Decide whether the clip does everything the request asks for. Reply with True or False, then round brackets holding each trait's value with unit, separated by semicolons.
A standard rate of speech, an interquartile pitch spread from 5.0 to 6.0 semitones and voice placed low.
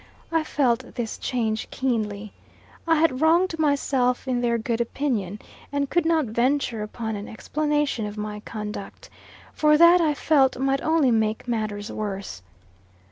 False (145 wpm; 5.4 semitones; 245 Hz)